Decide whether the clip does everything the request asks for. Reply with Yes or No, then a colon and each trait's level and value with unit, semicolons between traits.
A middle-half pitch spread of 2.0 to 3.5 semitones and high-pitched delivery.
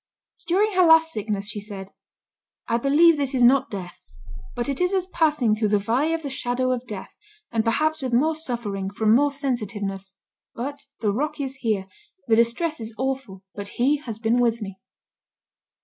No: average, 5.3 semitones; high, 245 Hz